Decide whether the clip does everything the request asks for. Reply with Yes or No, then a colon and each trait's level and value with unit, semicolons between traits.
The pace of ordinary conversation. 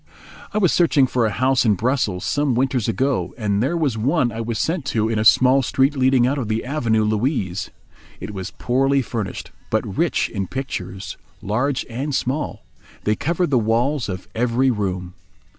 Yes: average, 180 wpm